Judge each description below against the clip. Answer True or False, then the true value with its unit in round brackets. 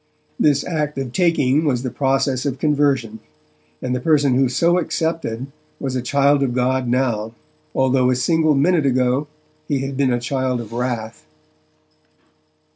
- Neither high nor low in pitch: False (130 Hz)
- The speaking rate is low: False (155 wpm)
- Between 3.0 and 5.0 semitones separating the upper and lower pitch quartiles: False (2.5 semitones)